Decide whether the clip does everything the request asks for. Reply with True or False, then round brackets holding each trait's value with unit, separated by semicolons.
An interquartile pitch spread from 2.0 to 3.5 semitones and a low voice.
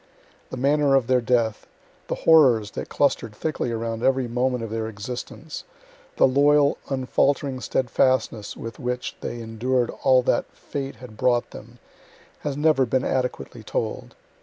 True (2.8 semitones; 125 Hz)